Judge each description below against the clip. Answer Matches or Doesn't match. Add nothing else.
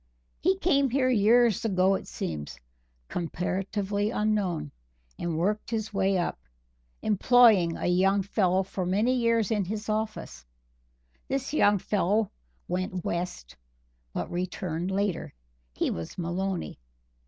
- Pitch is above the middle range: Matches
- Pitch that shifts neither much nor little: Matches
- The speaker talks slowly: Matches